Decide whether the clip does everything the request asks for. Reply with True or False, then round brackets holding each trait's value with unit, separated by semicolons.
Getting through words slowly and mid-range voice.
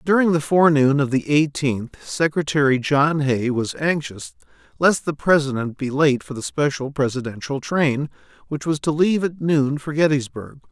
False (160 wpm; 145 Hz)